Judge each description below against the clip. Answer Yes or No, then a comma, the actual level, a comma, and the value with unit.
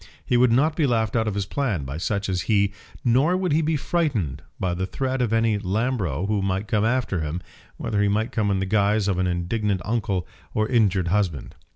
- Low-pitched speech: Yes, low, 105 Hz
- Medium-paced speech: No, fast, 215 wpm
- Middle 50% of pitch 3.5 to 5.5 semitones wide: Yes, average, 4.2 semitones